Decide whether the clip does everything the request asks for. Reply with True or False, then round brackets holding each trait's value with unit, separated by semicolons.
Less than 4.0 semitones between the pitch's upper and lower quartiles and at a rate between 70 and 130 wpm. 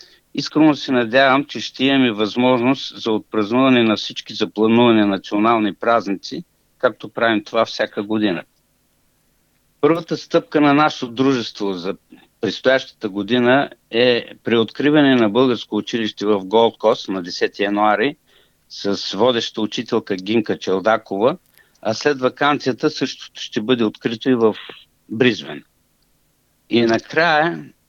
True (3.5 semitones; 120 wpm)